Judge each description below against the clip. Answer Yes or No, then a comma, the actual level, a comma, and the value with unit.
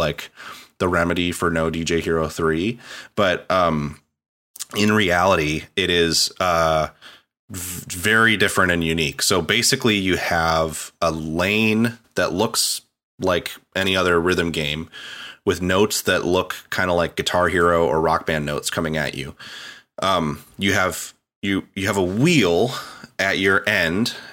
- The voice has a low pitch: Yes, very low, 85 Hz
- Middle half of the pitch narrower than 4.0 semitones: Yes, average, 2.8 semitones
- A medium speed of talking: Yes, average, 150 wpm